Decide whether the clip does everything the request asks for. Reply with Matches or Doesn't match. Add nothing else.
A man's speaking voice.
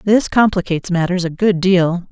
Doesn't match